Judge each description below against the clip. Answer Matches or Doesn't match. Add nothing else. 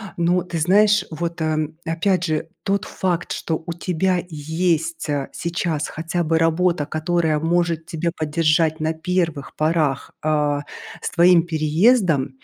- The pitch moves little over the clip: Matches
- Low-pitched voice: Doesn't match